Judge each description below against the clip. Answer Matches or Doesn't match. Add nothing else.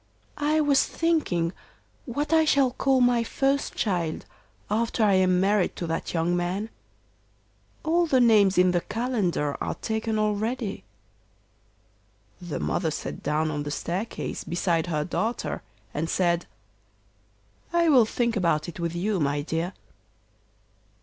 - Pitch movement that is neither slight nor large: Doesn't match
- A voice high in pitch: Matches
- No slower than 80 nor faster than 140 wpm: Matches